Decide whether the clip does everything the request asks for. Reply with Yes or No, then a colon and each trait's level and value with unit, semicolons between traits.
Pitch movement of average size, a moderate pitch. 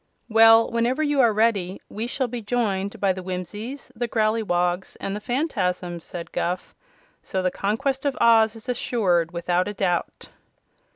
No: average, 4.4 semitones; high, 215 Hz